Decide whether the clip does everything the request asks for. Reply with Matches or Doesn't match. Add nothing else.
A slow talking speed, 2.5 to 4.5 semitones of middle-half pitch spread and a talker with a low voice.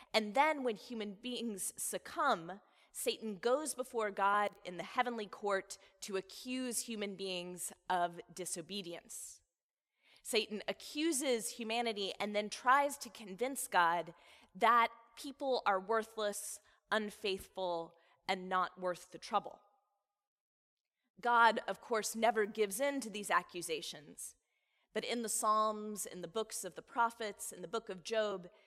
Doesn't match